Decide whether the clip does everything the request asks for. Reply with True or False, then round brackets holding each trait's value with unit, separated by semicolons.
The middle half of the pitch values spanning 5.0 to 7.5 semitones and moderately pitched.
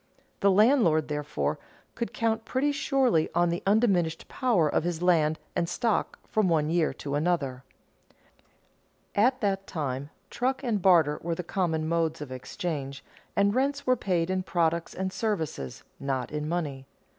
True (5.4 semitones; 175 Hz)